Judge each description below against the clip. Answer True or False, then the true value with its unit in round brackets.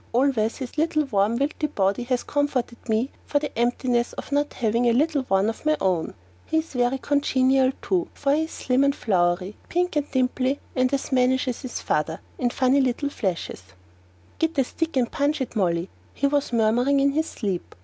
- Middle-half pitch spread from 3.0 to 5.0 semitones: True (3.7 semitones)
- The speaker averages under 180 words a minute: False (190 wpm)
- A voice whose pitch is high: True (255 Hz)